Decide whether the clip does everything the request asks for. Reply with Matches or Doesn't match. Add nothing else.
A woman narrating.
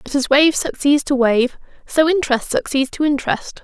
Matches